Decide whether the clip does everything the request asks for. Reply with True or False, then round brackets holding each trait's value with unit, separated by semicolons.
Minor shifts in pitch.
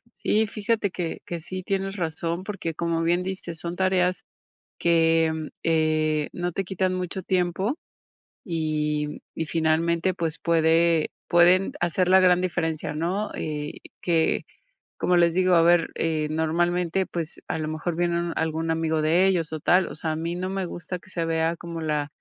True (2.1 semitones)